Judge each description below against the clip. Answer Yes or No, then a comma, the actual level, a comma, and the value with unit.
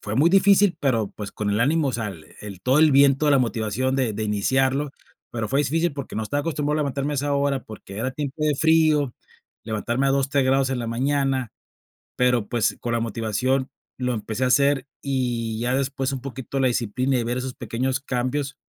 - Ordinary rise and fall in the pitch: Yes, average, 3.1 semitones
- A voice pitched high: No, low, 130 Hz